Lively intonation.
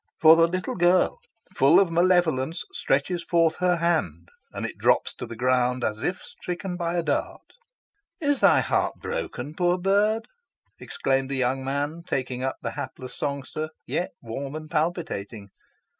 No: average, 5.0 semitones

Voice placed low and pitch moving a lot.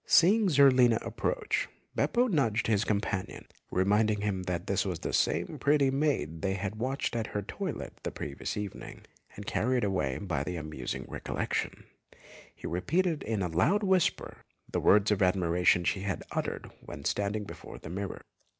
Yes: low, 105 Hz; wide, 6.4 semitones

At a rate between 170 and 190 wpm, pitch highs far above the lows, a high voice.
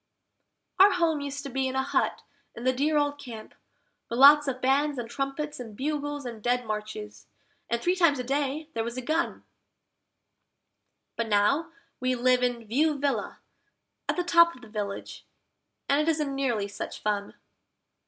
No: average, 175 wpm; average, 4.0 semitones; very high, 270 Hz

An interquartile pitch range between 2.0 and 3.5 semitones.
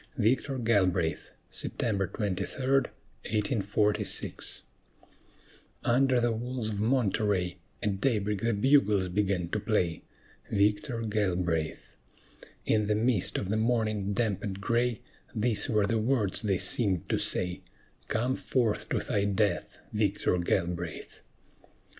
Yes: average, 2.9 semitones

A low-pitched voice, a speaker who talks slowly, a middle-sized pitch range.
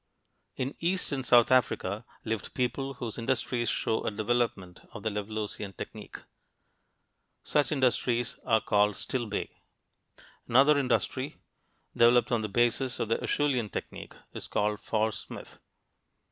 Yes: low, 120 Hz; slow, 125 wpm; average, 3.2 semitones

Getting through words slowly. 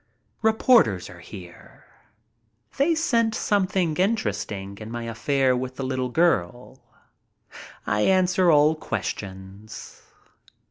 Yes: slow, 100 wpm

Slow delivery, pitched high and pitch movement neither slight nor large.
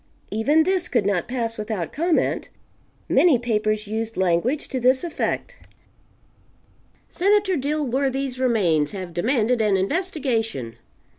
No: slow, 115 wpm; high, 240 Hz; wide, 5.7 semitones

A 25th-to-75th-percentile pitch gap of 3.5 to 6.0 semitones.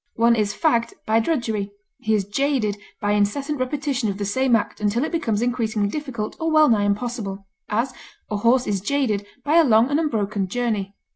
Yes: average, 4.5 semitones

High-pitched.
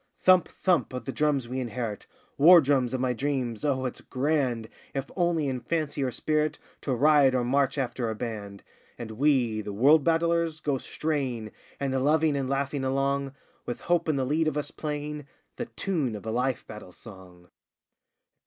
No: low, 135 Hz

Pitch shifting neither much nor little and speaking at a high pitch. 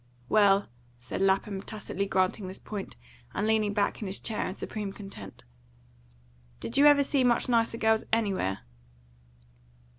No: narrow, 2.3 semitones; high, 205 Hz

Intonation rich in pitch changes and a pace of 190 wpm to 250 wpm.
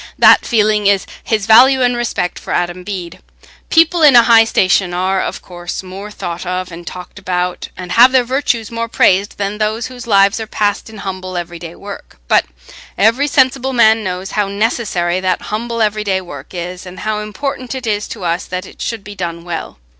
No: average, 3.9 semitones; average, 195 wpm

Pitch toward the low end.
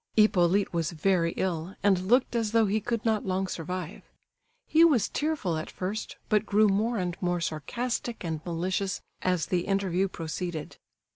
No: high, 190 Hz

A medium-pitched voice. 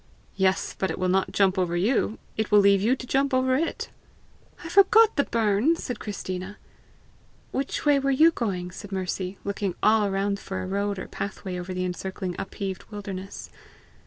No: high, 200 Hz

